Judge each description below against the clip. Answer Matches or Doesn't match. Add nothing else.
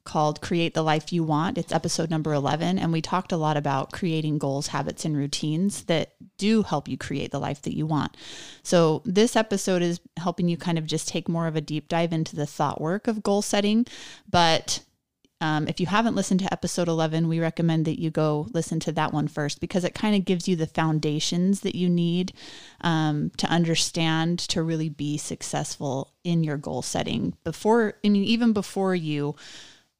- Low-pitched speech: Doesn't match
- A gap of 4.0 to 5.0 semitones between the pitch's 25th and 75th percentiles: Doesn't match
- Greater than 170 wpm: Matches